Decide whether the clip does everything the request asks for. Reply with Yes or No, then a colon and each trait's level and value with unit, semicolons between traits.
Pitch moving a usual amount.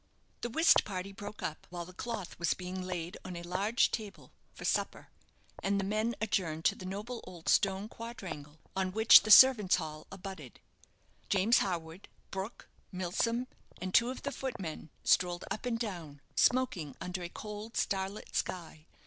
Yes: average, 3.8 semitones